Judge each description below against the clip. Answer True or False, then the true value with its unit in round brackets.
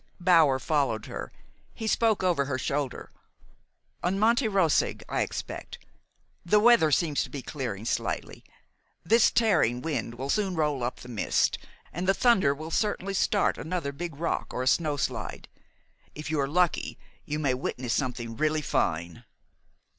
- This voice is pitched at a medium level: True (155 Hz)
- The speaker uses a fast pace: False (155 wpm)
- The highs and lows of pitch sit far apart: True (5.9 semitones)